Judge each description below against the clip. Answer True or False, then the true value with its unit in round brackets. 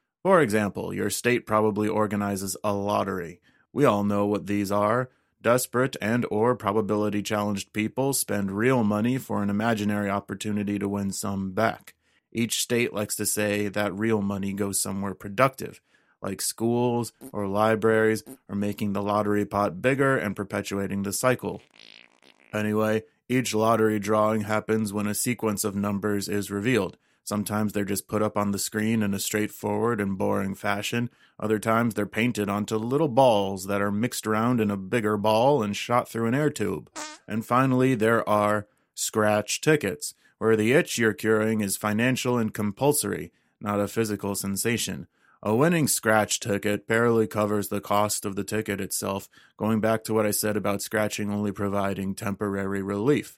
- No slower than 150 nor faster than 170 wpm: True (165 wpm)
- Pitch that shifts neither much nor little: False (1.7 semitones)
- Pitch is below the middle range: True (105 Hz)